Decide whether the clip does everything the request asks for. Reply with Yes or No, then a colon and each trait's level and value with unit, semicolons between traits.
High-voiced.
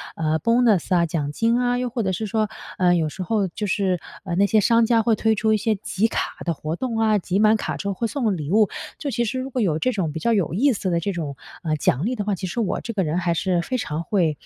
Yes: high, 200 Hz